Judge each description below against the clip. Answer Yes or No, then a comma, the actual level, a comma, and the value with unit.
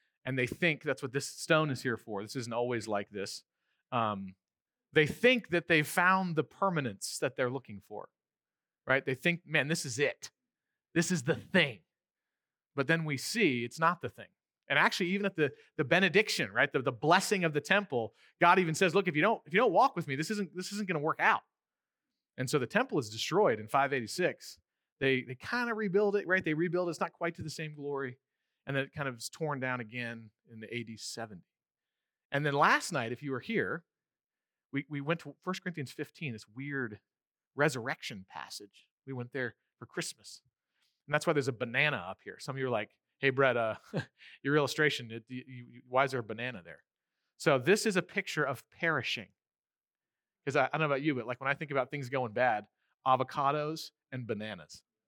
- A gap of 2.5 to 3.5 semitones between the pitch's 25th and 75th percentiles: No, average, 5.1 semitones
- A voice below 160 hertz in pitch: Yes, medium, 140 Hz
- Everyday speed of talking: No, fast, 210 wpm